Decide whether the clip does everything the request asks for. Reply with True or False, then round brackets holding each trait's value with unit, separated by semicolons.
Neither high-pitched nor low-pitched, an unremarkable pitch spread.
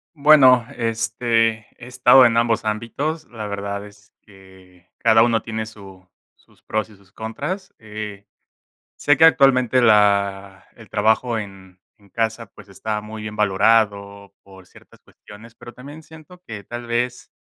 False (110 Hz; 3.0 semitones)